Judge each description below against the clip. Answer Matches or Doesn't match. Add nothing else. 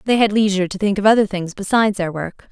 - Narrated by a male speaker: Doesn't match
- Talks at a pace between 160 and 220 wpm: Doesn't match